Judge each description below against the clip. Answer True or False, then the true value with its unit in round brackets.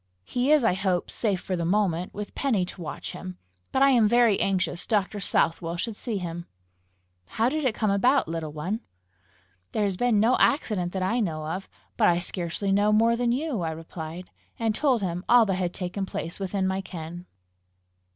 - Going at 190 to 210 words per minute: True (195 wpm)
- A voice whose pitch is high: True (195 Hz)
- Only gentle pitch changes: False (4.4 semitones)